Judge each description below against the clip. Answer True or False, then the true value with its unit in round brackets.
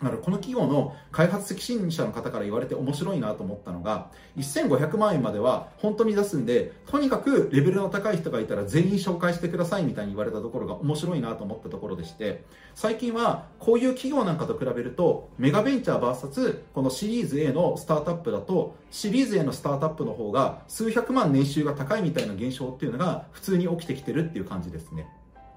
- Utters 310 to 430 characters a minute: False (440 characters per minute)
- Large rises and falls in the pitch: True (7.6 semitones)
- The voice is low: False (170 Hz)